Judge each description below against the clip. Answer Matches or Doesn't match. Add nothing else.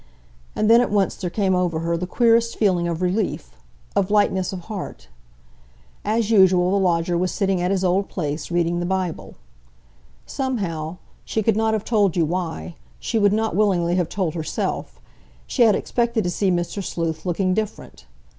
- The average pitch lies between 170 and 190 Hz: Matches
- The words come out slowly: Doesn't match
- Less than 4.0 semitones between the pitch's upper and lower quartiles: Matches